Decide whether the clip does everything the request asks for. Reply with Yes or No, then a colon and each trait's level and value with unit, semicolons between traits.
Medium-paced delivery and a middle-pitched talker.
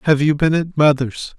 No: fast, 215 wpm; medium, 150 Hz